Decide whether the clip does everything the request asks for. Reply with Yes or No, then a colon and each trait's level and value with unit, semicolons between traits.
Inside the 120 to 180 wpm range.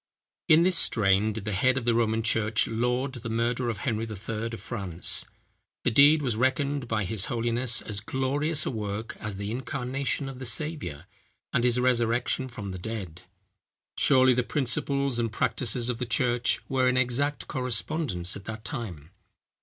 Yes: average, 170 wpm